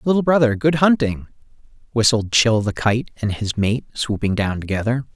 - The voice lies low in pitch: Yes, low, 115 Hz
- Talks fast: No, average, 165 wpm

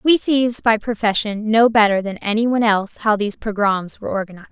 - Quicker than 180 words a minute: Yes, average, 200 wpm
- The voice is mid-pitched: No, high, 215 Hz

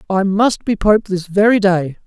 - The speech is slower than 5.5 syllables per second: Yes, 4.5 syllables/s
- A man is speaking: Yes, male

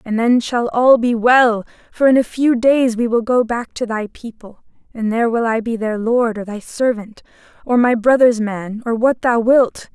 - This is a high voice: Yes, high, 235 Hz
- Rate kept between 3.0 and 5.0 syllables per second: Yes, 4.5 syllables/s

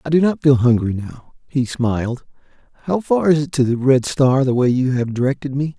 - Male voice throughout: Yes, male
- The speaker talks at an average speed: No, fast, 230 wpm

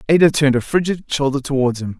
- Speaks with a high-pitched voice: No, medium, 140 Hz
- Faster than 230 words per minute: No, fast, 210 wpm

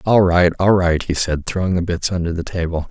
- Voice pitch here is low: Yes, very low, 90 Hz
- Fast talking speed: Yes, fast, 250 wpm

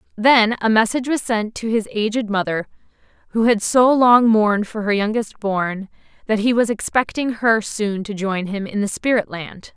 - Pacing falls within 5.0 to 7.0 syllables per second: No, 4.8 syllables/s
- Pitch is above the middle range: Yes, high, 220 Hz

